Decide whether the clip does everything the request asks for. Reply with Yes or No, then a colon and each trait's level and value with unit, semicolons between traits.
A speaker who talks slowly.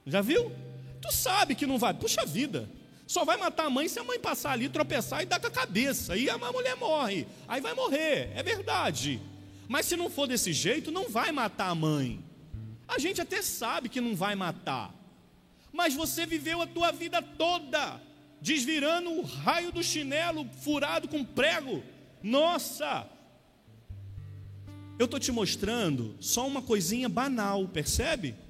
No: average, 165 wpm